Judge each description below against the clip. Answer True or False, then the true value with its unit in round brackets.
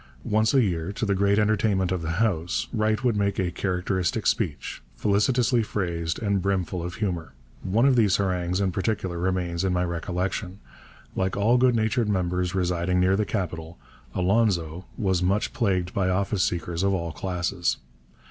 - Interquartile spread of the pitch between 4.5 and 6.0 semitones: False (2.9 semitones)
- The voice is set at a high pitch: False (95 Hz)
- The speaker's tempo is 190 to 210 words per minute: False (165 wpm)